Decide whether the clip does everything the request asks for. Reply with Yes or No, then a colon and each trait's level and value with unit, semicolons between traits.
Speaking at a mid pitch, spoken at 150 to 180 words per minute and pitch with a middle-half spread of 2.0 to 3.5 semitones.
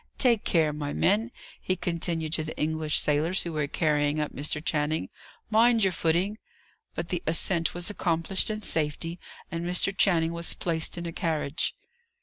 Yes: medium, 165 Hz; average, 165 wpm; average, 2.8 semitones